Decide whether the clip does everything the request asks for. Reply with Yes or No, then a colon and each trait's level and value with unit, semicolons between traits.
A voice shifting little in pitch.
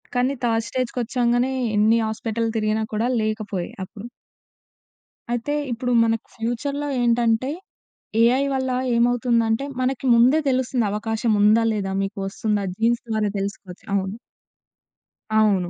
Yes: narrow, 2.3 semitones